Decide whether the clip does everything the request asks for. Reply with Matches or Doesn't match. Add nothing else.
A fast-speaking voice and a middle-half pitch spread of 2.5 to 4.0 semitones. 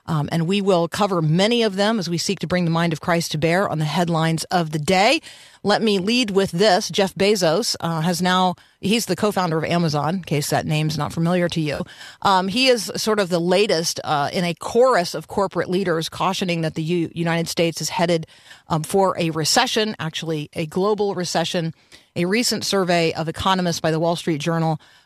Matches